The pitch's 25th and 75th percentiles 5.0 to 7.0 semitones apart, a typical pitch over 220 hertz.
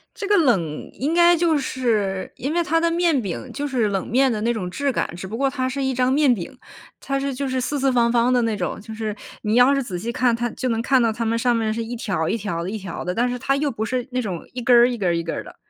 No: average, 3.8 semitones; high, 245 Hz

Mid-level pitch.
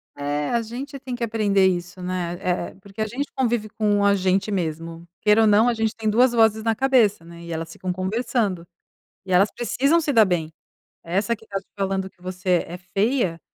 No: high, 200 Hz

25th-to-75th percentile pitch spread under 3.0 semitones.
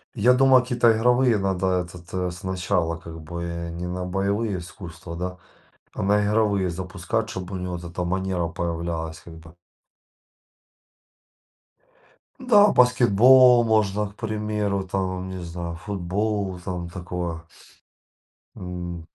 No: average, 3.3 semitones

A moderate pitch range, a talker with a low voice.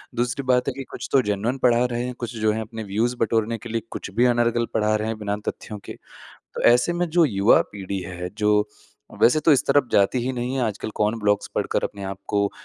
Yes: average, 3.0 semitones; low, 115 Hz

